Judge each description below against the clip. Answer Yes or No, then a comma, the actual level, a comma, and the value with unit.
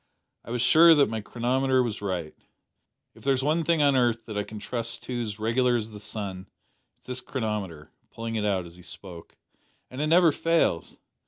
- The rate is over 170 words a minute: Yes, average, 200 wpm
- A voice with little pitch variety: No, average, 4.2 semitones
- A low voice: Yes, low, 115 Hz